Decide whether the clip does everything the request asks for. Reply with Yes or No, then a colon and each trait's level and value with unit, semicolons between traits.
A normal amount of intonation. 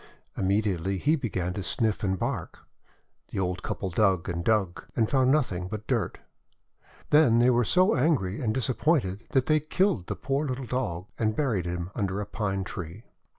No: wide, 5.7 semitones